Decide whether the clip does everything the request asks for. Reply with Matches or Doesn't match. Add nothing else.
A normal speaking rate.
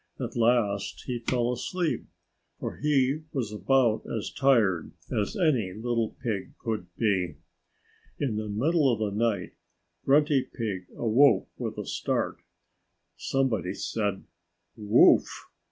Doesn't match